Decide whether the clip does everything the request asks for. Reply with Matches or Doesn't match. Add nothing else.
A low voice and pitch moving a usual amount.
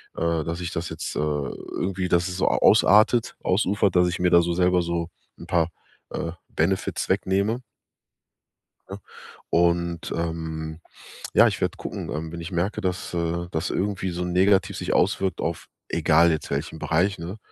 Doesn't match